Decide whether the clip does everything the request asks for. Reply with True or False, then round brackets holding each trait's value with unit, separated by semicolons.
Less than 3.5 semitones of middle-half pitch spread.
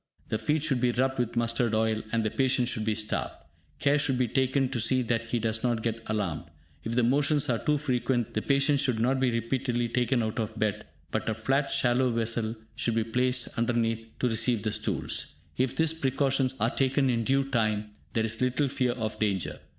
True (2.9 semitones)